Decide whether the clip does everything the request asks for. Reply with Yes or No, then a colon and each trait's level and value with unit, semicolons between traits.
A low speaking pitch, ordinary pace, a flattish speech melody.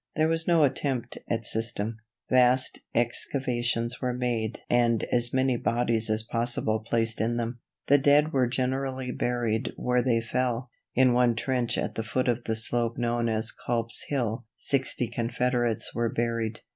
Yes: low, 120 Hz; average, 160 wpm; narrow, 1.7 semitones